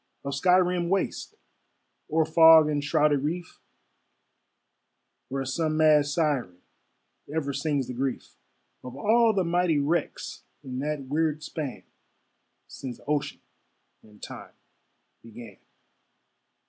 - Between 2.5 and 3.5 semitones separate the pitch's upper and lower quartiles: Yes, average, 3.1 semitones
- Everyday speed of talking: No, slow, 110 wpm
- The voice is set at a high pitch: No, medium, 150 Hz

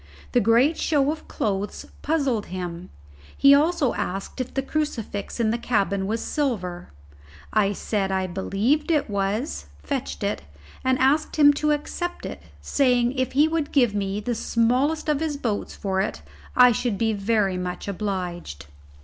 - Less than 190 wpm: Yes, average, 160 wpm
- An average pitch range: No, wide, 6.2 semitones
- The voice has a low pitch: No, high, 230 Hz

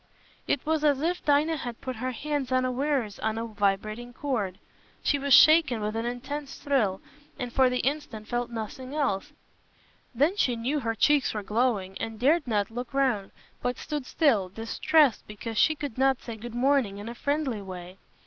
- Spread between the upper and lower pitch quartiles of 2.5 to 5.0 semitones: Yes, average, 4.5 semitones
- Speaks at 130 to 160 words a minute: No, average, 180 wpm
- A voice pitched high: Yes, high, 245 Hz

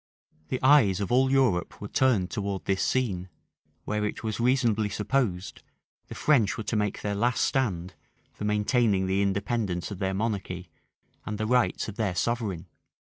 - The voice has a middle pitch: No, low, 105 Hz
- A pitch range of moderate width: Yes, average, 3.8 semitones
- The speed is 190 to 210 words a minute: No, average, 165 wpm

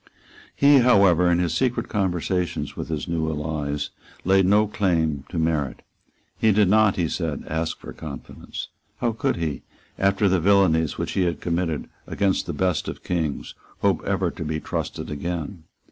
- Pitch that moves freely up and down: No, average, 3.6 semitones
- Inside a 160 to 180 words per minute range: Yes, average, 165 wpm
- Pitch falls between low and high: No, very low, 85 Hz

